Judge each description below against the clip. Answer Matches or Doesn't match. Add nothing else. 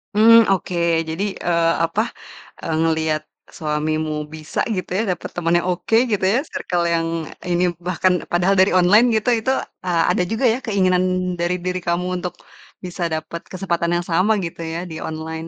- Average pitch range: Doesn't match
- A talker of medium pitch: Matches